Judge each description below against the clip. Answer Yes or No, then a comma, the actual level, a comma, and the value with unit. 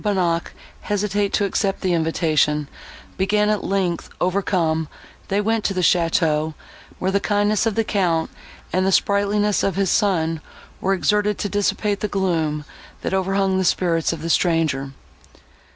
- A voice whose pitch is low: No, high, 190 Hz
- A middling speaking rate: Yes, average, 150 wpm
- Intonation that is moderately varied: Yes, average, 3.6 semitones